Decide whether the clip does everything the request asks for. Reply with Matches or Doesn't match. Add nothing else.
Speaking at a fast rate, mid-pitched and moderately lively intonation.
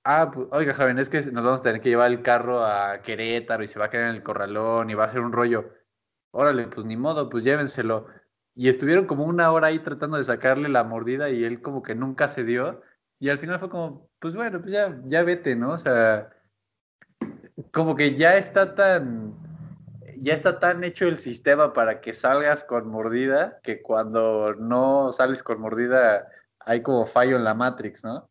Doesn't match